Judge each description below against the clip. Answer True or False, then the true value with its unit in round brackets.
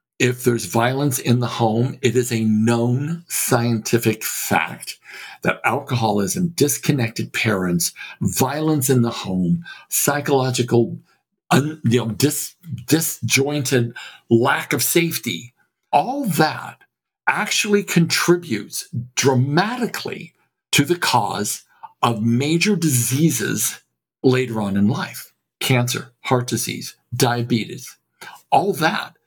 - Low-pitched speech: True (130 Hz)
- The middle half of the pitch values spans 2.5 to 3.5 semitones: False (4.5 semitones)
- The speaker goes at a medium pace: False (105 wpm)